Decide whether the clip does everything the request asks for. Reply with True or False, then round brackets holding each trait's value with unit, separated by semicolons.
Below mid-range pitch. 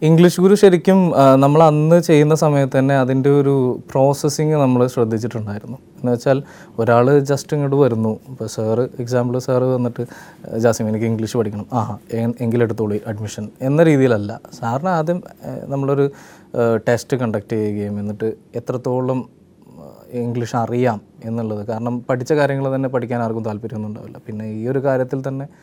True (125 Hz)